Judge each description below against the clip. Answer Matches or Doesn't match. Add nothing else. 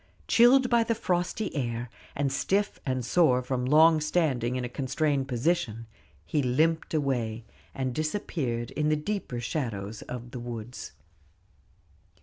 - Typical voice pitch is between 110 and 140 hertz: Matches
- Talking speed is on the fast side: Doesn't match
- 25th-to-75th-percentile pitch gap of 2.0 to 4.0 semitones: Doesn't match